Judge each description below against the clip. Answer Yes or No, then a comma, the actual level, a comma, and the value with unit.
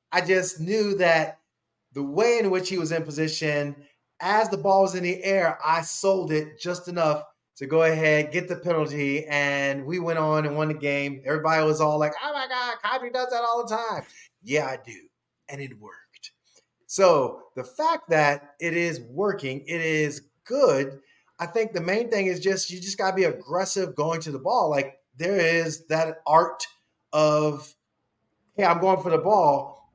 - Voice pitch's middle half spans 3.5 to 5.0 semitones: Yes, average, 4.2 semitones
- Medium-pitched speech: Yes, medium, 165 Hz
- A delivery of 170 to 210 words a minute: Yes, average, 195 wpm